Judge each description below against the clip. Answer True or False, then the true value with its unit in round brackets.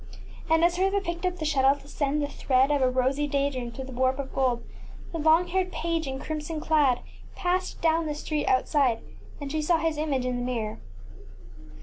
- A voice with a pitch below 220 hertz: False (295 Hz)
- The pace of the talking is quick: True (210 wpm)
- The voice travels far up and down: False (3.7 semitones)